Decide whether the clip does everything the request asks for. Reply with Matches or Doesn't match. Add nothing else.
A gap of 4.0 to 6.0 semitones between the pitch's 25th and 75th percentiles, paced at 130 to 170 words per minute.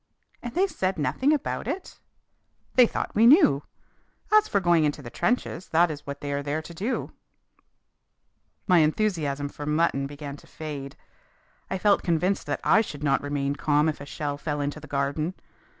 Doesn't match